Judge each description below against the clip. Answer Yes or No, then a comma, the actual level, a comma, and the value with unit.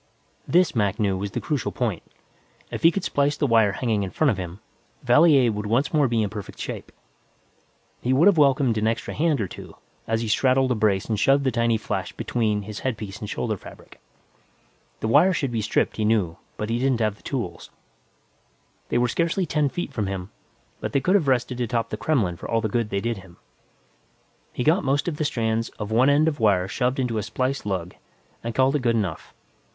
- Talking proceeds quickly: Yes, fast, 210 wpm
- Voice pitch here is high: No, low, 115 Hz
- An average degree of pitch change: Yes, average, 4.5 semitones